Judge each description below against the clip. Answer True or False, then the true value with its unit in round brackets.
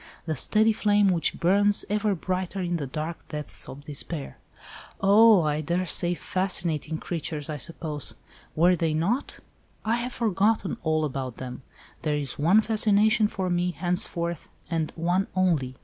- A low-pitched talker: False (175 Hz)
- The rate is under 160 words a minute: True (140 wpm)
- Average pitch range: True (4.5 semitones)